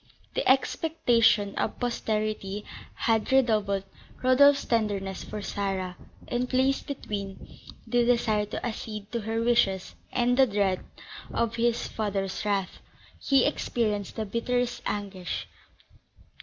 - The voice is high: Yes, high, 220 Hz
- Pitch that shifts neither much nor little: Yes, average, 3.4 semitones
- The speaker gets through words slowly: Yes, slow, 115 wpm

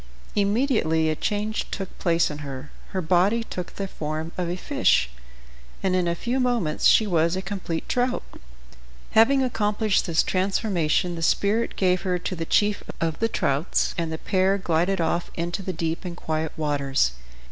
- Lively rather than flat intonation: No, average, 4.1 semitones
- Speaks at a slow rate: No, average, 170 wpm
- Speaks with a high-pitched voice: No, medium, 180 Hz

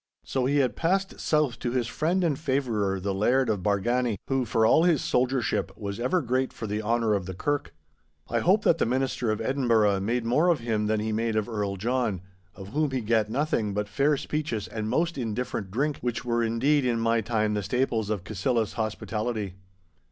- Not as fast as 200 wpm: No, fast, 205 wpm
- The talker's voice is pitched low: Yes, low, 115 Hz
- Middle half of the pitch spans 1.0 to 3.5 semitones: No, average, 3.9 semitones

